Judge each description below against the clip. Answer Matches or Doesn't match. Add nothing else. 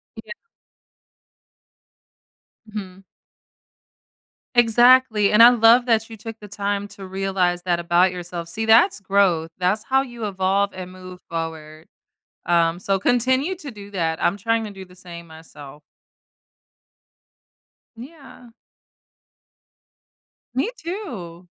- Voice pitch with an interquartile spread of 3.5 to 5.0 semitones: Matches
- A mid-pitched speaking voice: Doesn't match